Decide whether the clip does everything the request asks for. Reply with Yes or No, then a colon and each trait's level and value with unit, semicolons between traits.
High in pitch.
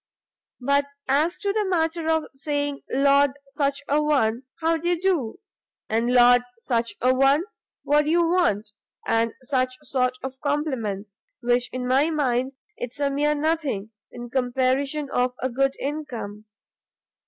Yes: very high, 275 Hz